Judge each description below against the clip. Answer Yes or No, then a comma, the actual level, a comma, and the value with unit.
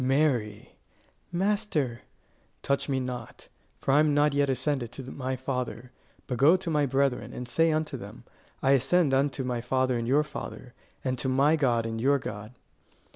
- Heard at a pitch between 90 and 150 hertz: Yes, low, 135 Hz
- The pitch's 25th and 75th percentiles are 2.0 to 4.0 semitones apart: Yes, average, 2.9 semitones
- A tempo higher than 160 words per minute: Yes, average, 175 wpm